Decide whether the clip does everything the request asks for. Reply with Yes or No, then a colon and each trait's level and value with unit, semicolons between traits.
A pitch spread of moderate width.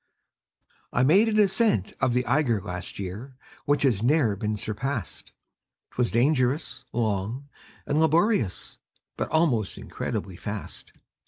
No: wide, 6.0 semitones